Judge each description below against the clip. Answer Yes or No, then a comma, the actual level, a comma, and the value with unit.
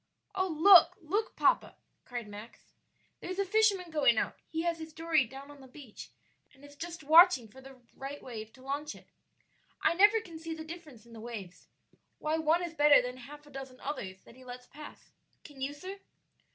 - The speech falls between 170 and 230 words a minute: Yes, average, 200 wpm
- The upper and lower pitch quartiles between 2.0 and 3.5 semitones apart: No, average, 4.6 semitones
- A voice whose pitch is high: Yes, very high, 295 Hz